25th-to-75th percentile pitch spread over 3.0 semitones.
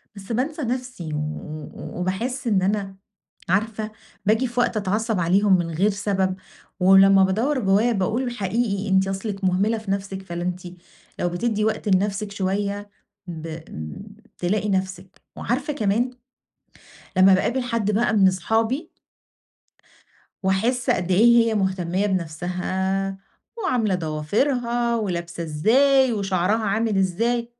Yes: average, 3.5 semitones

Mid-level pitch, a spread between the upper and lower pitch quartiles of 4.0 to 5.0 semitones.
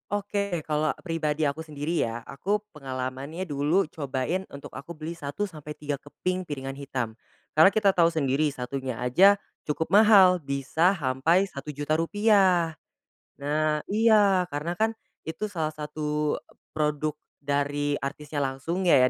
Yes: medium, 155 Hz; average, 4.3 semitones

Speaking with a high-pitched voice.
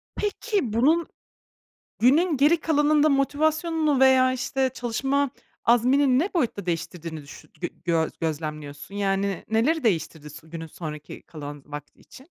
Yes: high, 245 Hz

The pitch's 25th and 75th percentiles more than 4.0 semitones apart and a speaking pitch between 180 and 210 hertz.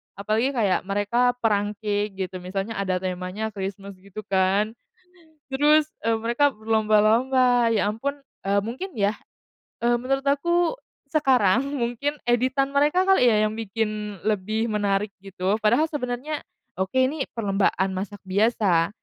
No: average, 4.5 semitones; high, 220 Hz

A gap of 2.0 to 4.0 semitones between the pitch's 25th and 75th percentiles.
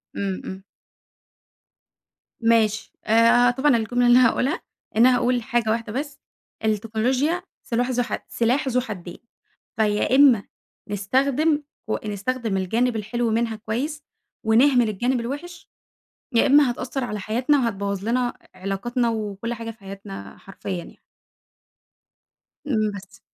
Yes: average, 3.1 semitones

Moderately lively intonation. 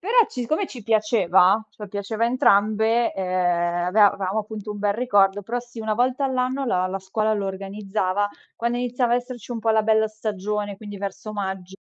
Yes: average, 3.2 semitones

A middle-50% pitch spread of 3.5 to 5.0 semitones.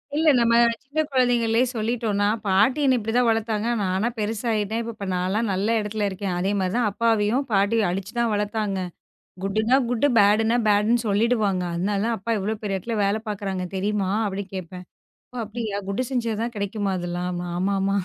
No: average, 2.8 semitones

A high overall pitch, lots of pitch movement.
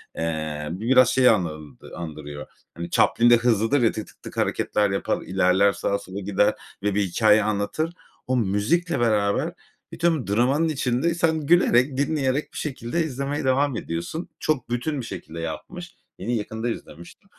No: low, 115 Hz; wide, 6.1 semitones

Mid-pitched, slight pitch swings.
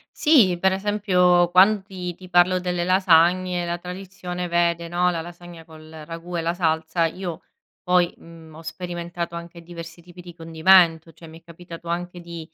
Yes: medium, 175 Hz; narrow, 1.4 semitones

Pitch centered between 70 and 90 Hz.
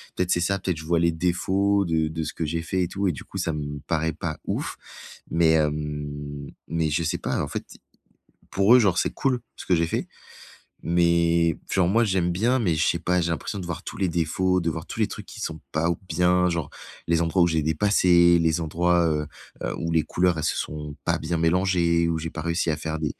Yes: very low, 85 Hz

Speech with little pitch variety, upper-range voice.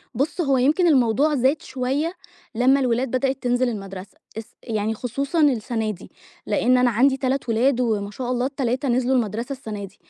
No: average, 3.2 semitones; very high, 250 Hz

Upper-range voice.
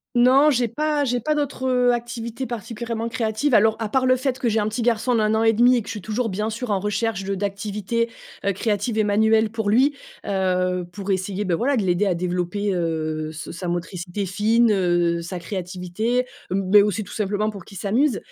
Yes: high, 215 Hz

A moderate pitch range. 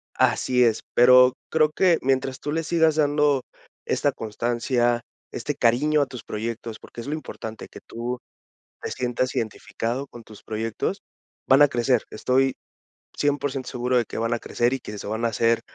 Yes: average, 3.2 semitones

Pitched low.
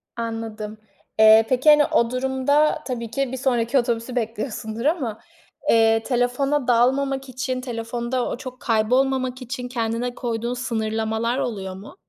No: high, 245 Hz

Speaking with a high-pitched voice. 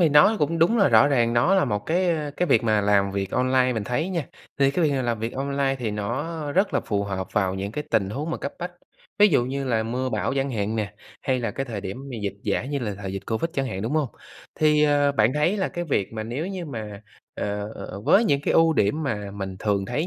No: low, 130 Hz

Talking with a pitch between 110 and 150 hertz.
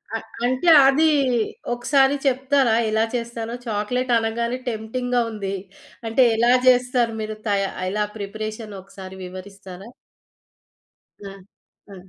No: high, 225 Hz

